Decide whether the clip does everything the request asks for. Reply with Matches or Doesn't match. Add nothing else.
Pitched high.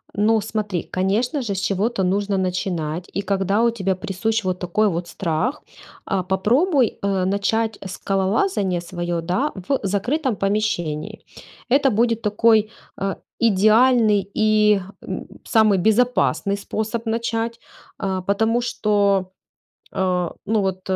Matches